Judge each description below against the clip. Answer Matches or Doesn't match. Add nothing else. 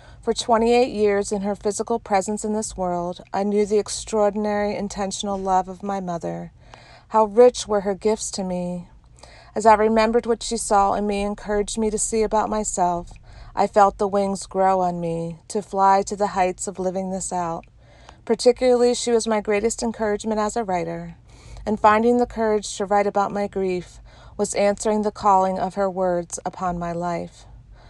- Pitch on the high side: Matches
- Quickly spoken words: Doesn't match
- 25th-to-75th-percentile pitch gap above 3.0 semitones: Doesn't match